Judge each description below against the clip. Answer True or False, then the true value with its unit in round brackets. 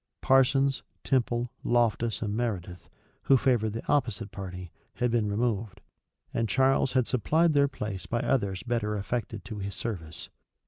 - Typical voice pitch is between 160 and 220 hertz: False (115 Hz)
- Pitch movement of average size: True (3.9 semitones)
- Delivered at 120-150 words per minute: True (145 wpm)